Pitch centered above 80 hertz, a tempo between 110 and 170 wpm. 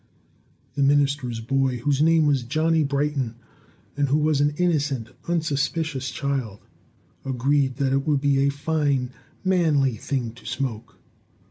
Yes: medium, 140 Hz; slow, 135 wpm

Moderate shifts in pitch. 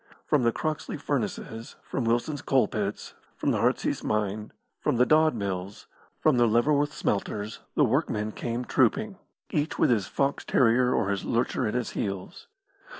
Yes: average, 4.6 semitones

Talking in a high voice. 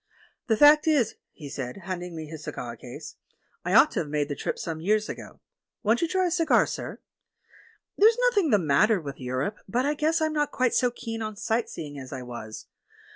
Yes: high, 210 Hz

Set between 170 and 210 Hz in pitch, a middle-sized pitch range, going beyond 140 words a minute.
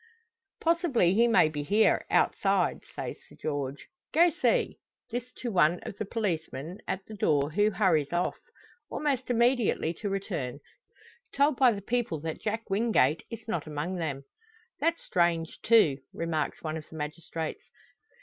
No: medium, 185 Hz; wide, 6.7 semitones; average, 150 wpm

